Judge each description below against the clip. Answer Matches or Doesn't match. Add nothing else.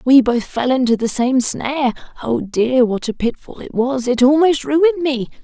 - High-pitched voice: Matches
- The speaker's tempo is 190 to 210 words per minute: Matches